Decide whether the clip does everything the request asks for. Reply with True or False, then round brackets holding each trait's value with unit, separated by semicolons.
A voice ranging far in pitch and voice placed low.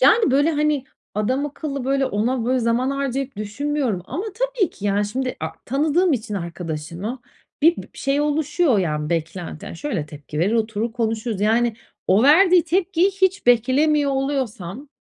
False (6.1 semitones; 260 Hz)